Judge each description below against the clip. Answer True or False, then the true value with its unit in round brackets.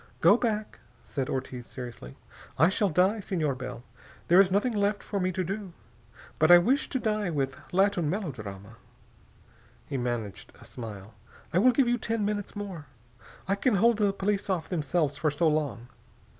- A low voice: False (180 Hz)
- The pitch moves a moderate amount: False (7.0 semitones)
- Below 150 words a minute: False (170 wpm)